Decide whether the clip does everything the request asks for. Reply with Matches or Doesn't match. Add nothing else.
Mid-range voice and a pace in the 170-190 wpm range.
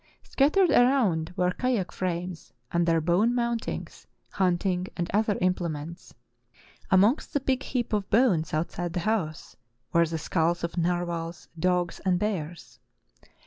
Doesn't match